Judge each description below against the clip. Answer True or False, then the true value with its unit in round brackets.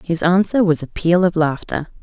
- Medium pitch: True (175 Hz)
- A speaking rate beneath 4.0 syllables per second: False (4.9 syllables/s)